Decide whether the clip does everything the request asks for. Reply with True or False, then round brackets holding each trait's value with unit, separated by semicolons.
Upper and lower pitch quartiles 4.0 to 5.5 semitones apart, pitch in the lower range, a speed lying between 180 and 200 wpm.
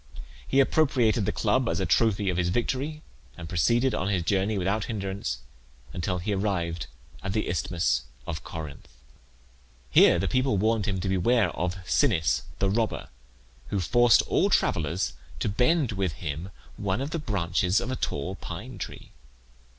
False (4.8 semitones; 95 Hz; 160 wpm)